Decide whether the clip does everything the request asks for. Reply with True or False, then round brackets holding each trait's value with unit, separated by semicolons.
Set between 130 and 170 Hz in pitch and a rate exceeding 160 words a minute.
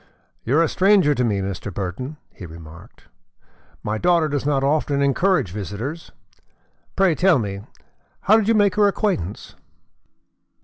False (140 Hz; 145 wpm)